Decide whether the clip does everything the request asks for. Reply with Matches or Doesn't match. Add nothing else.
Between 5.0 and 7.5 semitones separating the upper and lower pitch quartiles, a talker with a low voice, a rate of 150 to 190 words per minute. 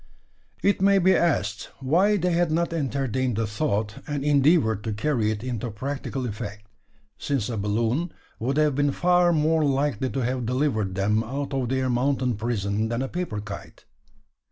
Matches